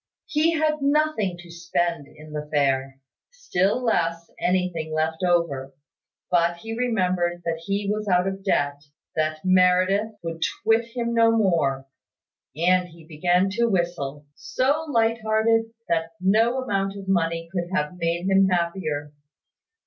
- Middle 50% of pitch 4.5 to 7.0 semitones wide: Yes, average, 4.8 semitones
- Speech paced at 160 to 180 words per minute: No, average, 140 wpm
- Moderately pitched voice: Yes, medium, 180 Hz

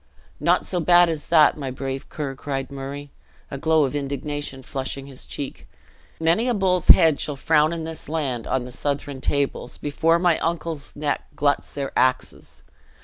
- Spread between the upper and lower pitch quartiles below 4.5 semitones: Yes, average, 3.0 semitones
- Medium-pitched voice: Yes, medium, 145 Hz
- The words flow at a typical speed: Yes, average, 170 wpm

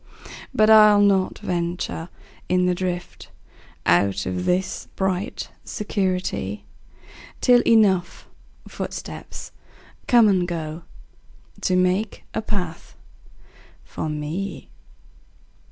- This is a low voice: No, medium, 180 Hz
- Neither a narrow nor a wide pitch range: Yes, average, 3.6 semitones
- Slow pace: Yes, slow, 80 wpm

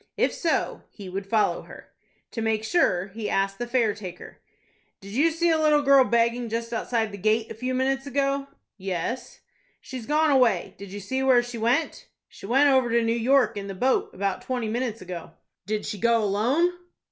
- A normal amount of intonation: Yes, average, 4.3 semitones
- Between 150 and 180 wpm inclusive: No, average, 195 wpm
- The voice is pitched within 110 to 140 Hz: No, high, 235 Hz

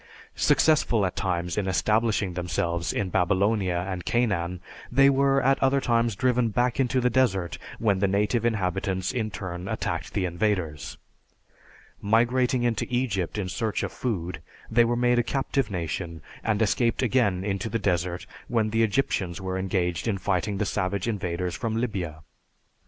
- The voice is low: Yes, low, 105 Hz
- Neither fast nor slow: Yes, average, 155 wpm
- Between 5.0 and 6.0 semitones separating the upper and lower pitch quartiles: No, average, 4.5 semitones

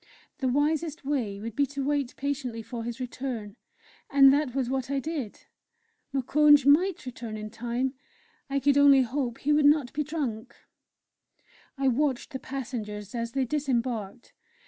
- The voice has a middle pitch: No, very high, 265 Hz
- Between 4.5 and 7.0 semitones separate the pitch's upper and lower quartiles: No, average, 3.3 semitones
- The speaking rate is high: No, average, 155 wpm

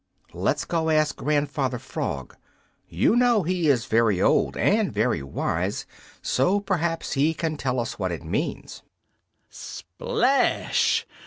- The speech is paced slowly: Yes, slow, 130 wpm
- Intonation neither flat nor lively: No, wide, 6.6 semitones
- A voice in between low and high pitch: Yes, medium, 150 Hz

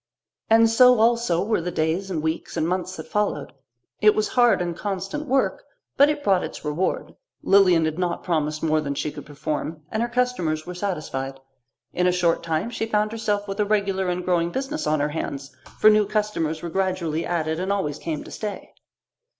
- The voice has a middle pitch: Yes, medium, 180 Hz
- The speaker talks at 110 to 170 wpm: No, average, 200 wpm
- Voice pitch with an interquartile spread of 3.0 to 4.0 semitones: No, average, 5.1 semitones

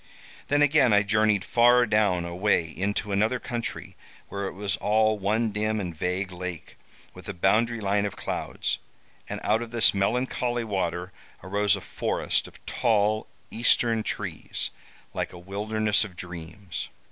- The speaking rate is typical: Yes, average, 150 wpm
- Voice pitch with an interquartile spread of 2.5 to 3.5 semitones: Yes, average, 2.8 semitones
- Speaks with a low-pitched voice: Yes, low, 105 Hz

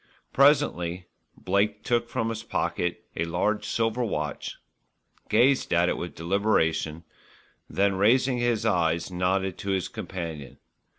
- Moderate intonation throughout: Yes, average, 4.8 semitones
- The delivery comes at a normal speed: No, slow, 125 wpm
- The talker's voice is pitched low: Yes, very low, 95 Hz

